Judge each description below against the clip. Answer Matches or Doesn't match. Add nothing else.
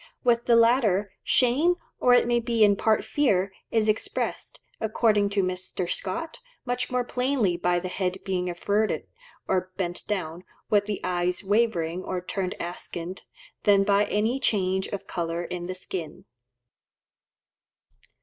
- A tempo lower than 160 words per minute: Matches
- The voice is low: Doesn't match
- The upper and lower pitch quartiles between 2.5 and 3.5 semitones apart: Doesn't match